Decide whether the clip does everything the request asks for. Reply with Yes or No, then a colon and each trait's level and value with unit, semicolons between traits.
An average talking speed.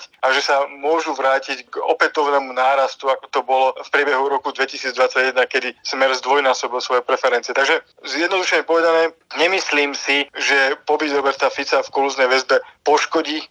Yes: average, 145 wpm